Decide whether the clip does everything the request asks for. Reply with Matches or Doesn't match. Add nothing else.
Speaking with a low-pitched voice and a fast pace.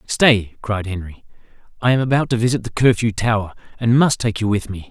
Matches